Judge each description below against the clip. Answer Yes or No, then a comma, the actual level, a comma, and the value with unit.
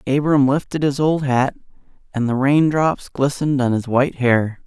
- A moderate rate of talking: Yes, average, 165 wpm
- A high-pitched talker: No, low, 135 Hz